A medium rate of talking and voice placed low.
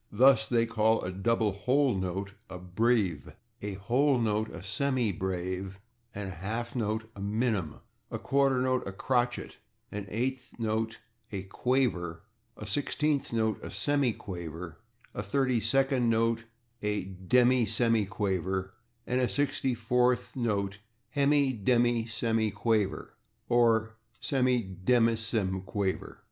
No: slow, 115 wpm; low, 110 Hz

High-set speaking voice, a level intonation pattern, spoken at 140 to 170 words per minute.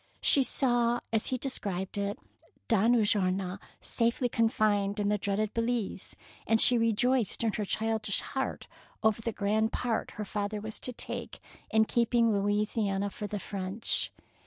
Yes: high, 215 Hz; narrow, 2.3 semitones; average, 150 wpm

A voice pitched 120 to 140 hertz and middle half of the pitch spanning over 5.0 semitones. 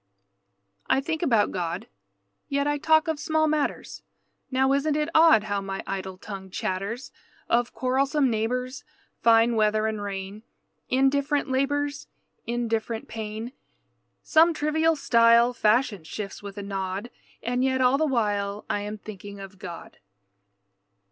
No: high, 235 Hz; wide, 5.4 semitones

